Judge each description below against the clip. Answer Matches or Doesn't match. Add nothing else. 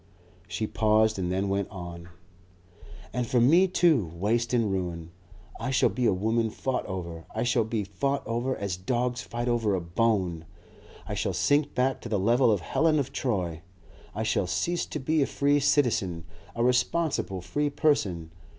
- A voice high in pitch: Doesn't match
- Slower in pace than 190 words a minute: Matches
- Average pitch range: Doesn't match